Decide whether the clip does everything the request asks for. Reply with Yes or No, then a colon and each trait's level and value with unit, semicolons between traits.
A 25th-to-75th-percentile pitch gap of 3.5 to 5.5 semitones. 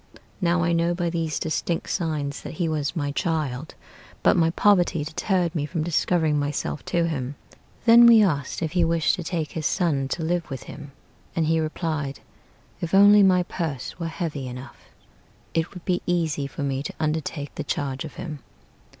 No: average, 3.0 semitones